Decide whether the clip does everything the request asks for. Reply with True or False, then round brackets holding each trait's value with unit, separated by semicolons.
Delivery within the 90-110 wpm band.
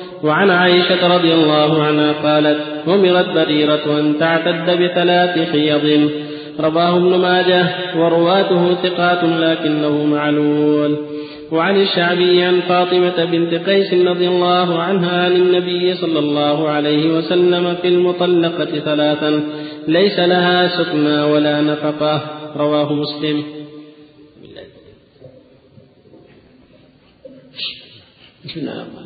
True (95 wpm)